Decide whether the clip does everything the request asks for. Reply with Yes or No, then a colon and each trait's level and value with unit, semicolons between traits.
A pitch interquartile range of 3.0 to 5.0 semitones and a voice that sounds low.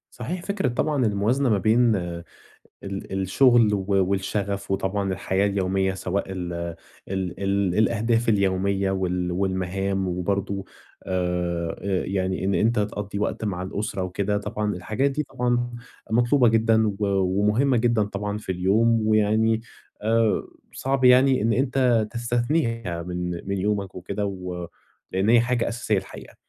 Yes: average, 3.4 semitones; low, 100 Hz